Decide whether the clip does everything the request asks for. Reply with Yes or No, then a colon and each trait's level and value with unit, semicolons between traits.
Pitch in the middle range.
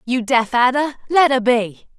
No: very high, 250 Hz